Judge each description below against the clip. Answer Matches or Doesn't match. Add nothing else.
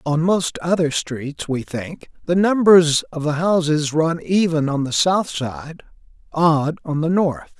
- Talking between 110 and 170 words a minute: Matches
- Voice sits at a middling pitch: Matches